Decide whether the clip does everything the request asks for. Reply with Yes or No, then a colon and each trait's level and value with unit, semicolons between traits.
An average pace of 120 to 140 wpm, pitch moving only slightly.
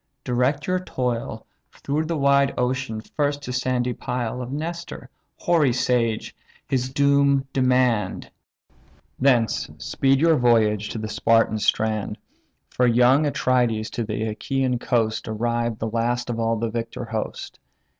No: slow, 135 wpm; average, 3.1 semitones